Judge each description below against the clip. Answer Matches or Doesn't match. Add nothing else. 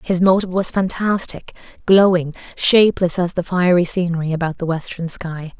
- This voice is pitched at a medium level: Matches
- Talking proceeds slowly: Doesn't match